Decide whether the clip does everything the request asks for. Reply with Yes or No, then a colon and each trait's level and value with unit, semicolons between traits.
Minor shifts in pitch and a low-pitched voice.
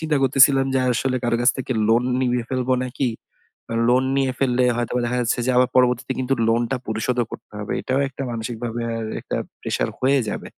Yes: narrow, 1.8 semitones; low, 125 Hz